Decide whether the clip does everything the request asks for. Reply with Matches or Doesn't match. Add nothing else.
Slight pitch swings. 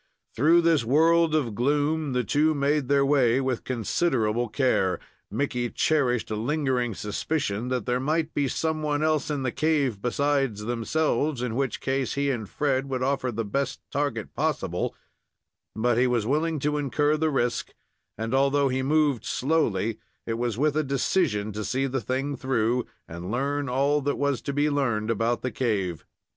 Doesn't match